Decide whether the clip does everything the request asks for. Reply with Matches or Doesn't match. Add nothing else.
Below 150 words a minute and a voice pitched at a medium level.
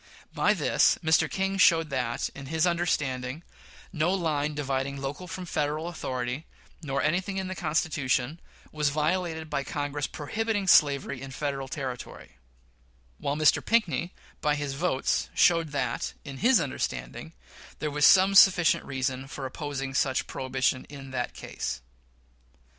Matches